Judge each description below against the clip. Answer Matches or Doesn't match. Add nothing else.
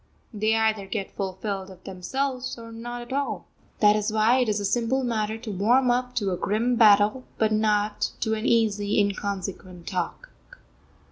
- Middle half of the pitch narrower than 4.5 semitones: Matches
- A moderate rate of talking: Matches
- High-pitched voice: Matches